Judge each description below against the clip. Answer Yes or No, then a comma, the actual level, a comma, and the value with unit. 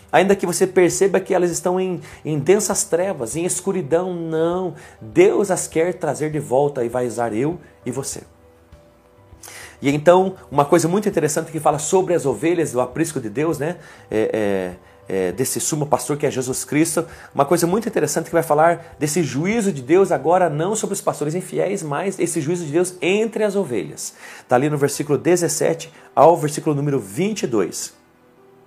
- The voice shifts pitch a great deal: No, average, 5.0 semitones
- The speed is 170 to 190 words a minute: Yes, average, 180 wpm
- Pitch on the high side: No, medium, 160 Hz